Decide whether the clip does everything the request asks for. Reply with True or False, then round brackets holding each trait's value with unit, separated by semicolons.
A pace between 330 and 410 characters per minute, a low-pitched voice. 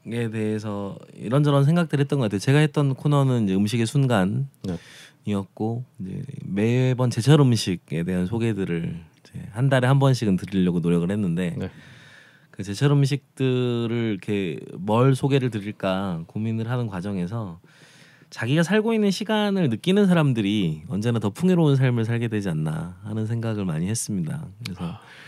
True (335 characters per minute; 115 Hz)